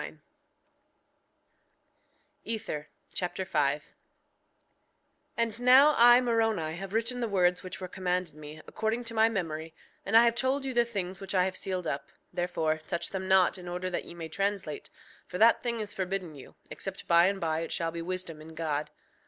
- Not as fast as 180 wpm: No, average, 185 wpm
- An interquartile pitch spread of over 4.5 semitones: Yes, average, 5.1 semitones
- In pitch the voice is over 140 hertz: Yes, medium, 185 Hz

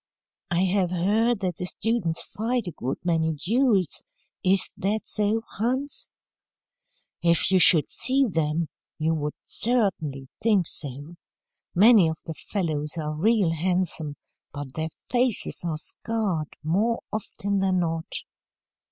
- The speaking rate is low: Yes, slow, 130 wpm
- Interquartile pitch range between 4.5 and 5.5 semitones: Yes, average, 5.1 semitones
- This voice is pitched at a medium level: Yes, medium, 180 Hz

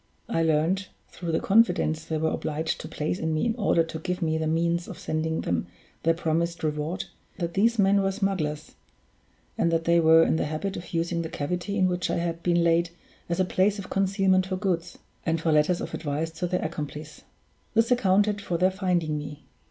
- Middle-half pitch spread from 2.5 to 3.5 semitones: Yes, average, 2.8 semitones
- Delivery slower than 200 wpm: No, fast, 205 wpm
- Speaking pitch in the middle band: Yes, medium, 170 Hz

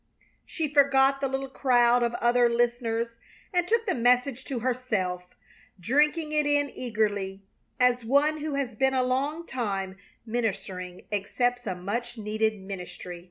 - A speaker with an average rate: Yes, average, 145 wpm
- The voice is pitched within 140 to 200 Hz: No, high, 245 Hz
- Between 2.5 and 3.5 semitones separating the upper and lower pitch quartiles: No, average, 4.2 semitones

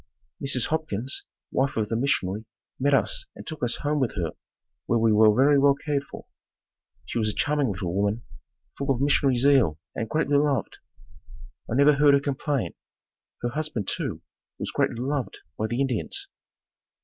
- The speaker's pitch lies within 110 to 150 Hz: Yes, low, 135 Hz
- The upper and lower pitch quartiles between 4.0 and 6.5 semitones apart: Yes, average, 4.3 semitones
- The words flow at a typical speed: Yes, average, 170 wpm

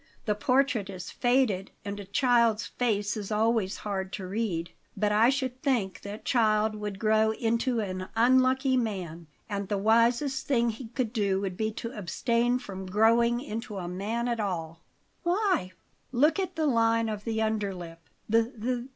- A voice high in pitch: Yes, high, 220 Hz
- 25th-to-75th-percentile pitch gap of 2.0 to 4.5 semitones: Yes, average, 3.3 semitones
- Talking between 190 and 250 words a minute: No, average, 165 wpm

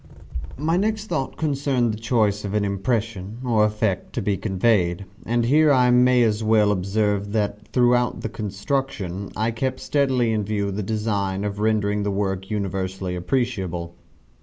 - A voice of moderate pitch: No, low, 105 Hz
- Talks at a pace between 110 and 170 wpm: Yes, average, 160 wpm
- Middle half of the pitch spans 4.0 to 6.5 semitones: No, average, 3.5 semitones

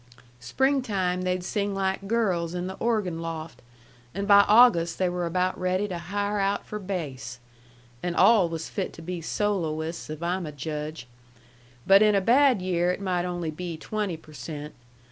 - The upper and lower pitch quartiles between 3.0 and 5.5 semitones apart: Yes, average, 3.4 semitones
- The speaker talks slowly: No, average, 175 wpm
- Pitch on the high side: No, medium, 180 Hz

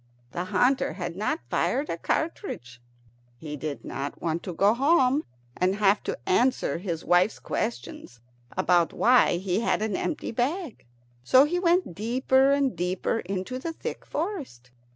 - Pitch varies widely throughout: Yes, wide, 7.6 semitones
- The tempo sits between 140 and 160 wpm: Yes, average, 155 wpm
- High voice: Yes, high, 205 Hz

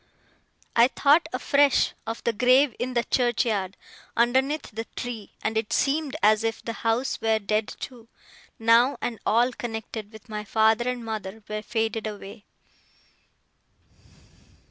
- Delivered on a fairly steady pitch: Yes, narrow, 2.3 semitones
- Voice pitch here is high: Yes, high, 225 Hz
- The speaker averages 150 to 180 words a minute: No, average, 140 wpm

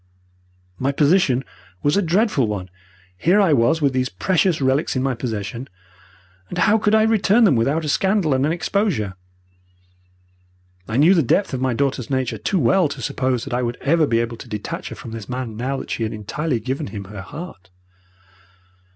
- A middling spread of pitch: No, wide, 6.2 semitones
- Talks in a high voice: No, low, 135 Hz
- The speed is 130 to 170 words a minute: No, average, 195 wpm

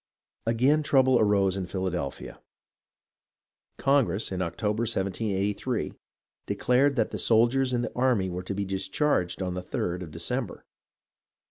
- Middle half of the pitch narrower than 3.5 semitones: No, average, 5.1 semitones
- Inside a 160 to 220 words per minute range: No, slow, 135 wpm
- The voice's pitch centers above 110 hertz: No, low, 105 Hz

